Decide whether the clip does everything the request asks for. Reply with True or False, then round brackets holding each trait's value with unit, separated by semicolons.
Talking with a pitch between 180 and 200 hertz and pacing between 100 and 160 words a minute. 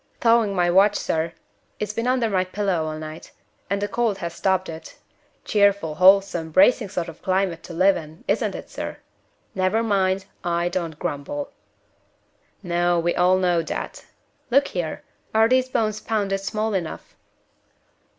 True (190 Hz; 155 wpm)